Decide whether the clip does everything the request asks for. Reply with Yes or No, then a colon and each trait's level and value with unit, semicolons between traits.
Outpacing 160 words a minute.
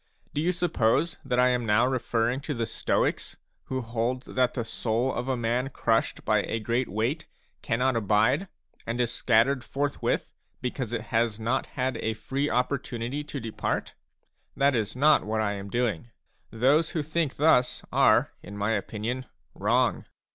Yes: average, 170 wpm